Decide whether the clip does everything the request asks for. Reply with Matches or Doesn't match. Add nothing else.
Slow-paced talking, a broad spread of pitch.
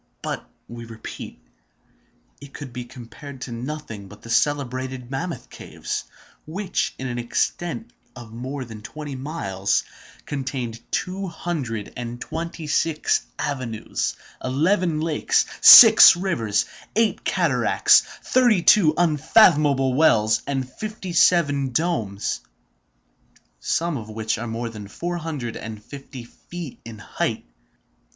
Matches